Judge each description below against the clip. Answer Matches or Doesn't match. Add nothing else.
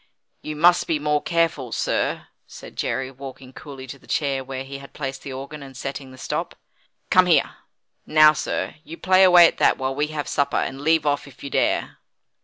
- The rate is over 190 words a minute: Matches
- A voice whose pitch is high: Doesn't match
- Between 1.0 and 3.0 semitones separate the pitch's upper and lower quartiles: Matches